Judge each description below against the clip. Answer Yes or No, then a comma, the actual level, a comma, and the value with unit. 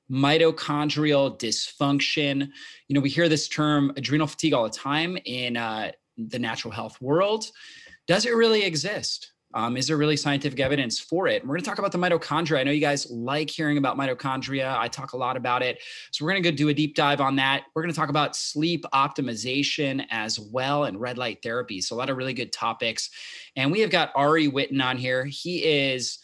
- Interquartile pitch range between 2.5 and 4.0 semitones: Yes, average, 2.9 semitones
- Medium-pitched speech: Yes, medium, 145 Hz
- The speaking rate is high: Yes, fast, 210 wpm